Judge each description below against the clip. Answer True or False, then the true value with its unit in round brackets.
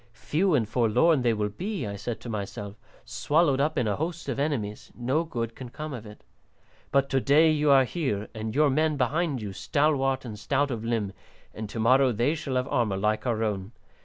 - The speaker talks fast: True (210 wpm)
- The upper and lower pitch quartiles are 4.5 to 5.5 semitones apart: True (5.2 semitones)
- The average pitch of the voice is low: True (125 Hz)